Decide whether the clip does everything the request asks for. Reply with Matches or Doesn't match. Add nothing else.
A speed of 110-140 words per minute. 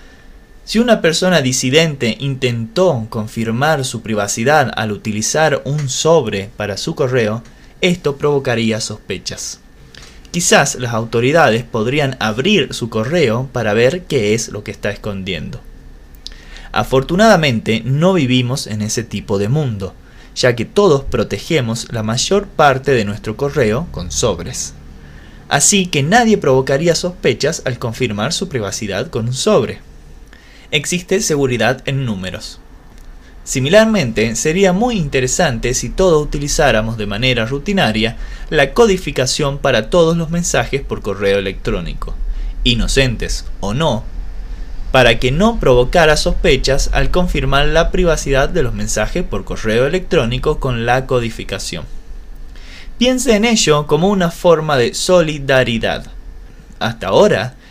Matches